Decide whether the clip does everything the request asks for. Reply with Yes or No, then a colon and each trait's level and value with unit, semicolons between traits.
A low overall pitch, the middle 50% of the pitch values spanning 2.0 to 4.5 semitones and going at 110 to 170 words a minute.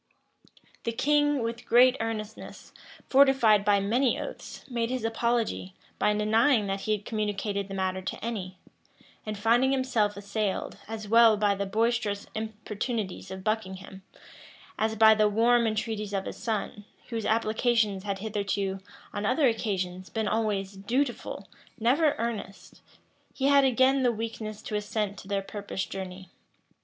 No: high, 215 Hz; narrow, 2.6 semitones; average, 145 wpm